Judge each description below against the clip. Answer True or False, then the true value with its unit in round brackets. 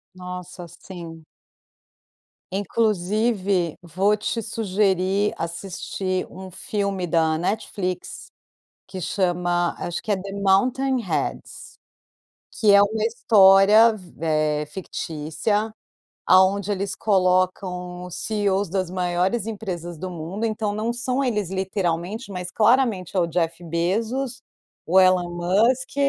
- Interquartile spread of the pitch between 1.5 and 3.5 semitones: True (3.2 semitones)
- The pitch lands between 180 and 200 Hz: True (190 Hz)